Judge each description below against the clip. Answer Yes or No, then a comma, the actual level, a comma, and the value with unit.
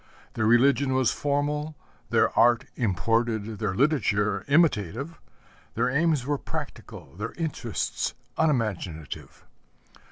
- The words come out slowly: Yes, slow, 100 wpm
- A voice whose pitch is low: Yes, low, 120 Hz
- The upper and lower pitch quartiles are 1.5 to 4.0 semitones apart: No, average, 5.2 semitones